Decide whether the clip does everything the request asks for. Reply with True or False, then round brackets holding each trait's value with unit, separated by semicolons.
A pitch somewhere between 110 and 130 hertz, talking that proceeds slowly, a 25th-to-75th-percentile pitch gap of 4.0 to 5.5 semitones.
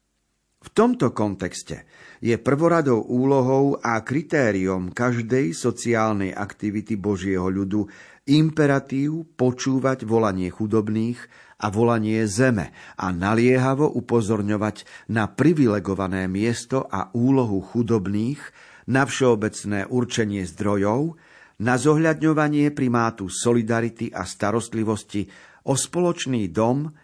True (115 Hz; 95 wpm; 4.3 semitones)